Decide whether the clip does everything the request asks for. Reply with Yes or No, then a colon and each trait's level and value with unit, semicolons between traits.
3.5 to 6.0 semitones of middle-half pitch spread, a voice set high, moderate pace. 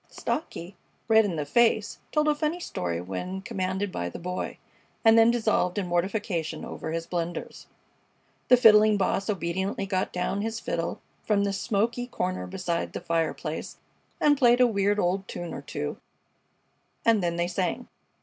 Yes: average, 4.4 semitones; high, 195 Hz; average, 160 wpm